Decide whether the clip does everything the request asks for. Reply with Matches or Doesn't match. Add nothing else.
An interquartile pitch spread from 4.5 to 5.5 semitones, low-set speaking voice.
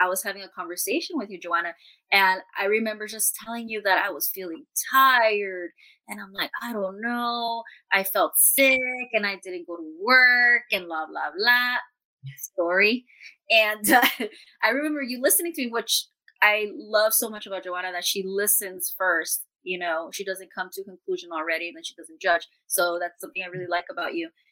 Doesn't match